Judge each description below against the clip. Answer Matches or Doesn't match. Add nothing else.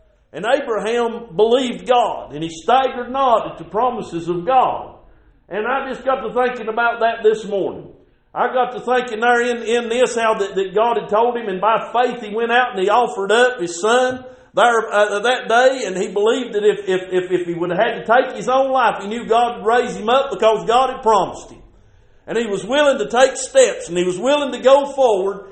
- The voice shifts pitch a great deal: Doesn't match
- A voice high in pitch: Matches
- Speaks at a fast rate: Matches